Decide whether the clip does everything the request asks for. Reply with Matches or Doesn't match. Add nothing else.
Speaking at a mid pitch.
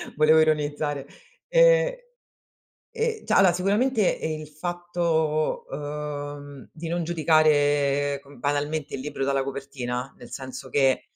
Matches